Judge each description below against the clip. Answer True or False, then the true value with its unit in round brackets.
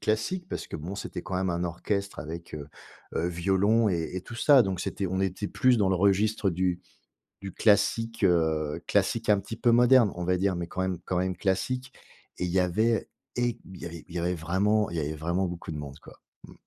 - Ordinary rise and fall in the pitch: True (3.8 semitones)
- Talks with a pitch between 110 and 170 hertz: False (95 Hz)